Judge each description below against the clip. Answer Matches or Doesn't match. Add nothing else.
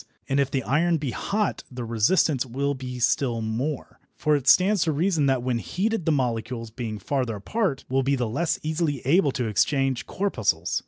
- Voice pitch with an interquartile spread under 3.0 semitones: Doesn't match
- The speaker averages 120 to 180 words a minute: Doesn't match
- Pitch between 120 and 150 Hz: Matches